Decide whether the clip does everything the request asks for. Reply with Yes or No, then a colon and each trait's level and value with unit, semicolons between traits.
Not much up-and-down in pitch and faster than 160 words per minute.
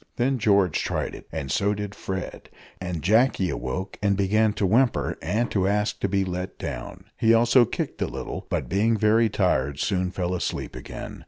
No: average, 3.2 semitones; average, 185 wpm